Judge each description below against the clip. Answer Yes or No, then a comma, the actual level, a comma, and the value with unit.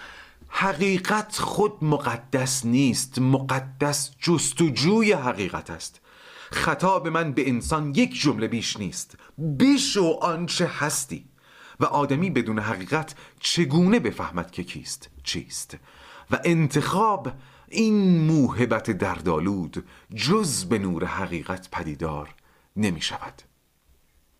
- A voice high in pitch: No, medium, 140 Hz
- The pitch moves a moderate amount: No, wide, 7.9 semitones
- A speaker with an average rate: No, slow, 100 wpm